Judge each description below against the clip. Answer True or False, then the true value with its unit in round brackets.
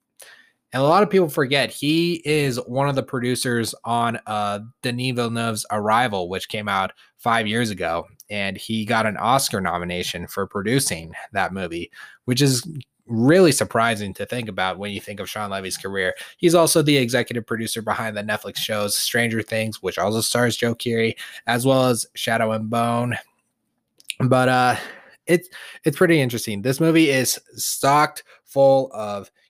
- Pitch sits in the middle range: False (115 Hz)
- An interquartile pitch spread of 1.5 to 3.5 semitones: False (4.1 semitones)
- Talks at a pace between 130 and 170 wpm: True (165 wpm)